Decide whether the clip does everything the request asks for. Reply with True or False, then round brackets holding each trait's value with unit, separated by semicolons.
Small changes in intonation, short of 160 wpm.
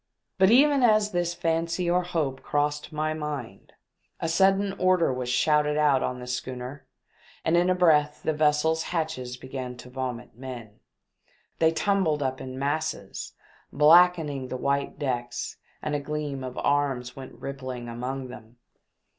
False (4.2 semitones; 150 wpm)